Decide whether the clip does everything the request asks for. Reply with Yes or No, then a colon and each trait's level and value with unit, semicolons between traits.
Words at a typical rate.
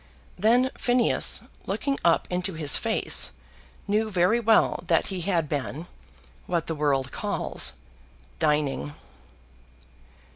No: slow, 110 wpm